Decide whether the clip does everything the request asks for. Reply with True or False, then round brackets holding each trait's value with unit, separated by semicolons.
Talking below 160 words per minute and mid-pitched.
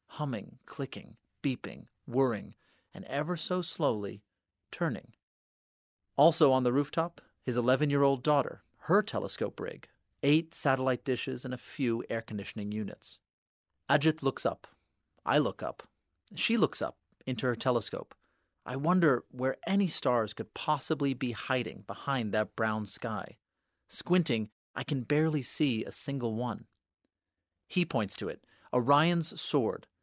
False (140 wpm; 130 Hz)